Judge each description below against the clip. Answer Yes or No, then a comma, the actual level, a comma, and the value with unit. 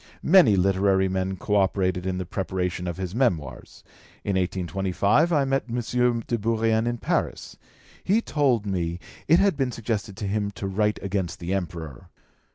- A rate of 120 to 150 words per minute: No, average, 165 wpm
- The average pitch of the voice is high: No, low, 100 Hz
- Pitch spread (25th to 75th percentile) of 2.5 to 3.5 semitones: No, average, 4.0 semitones